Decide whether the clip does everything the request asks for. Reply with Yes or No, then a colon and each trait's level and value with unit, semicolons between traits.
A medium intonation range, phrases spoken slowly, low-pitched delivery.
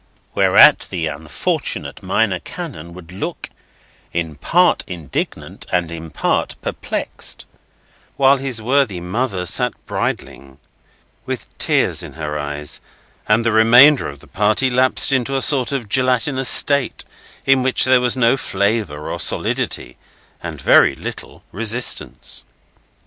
No: wide, 7.4 semitones; slow, 130 wpm; low, 110 Hz